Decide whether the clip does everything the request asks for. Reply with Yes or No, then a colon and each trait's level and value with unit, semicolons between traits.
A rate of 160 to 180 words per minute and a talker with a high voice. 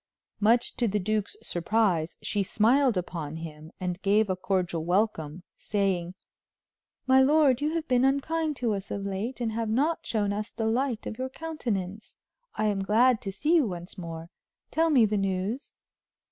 Yes: average, 175 wpm; high, 215 Hz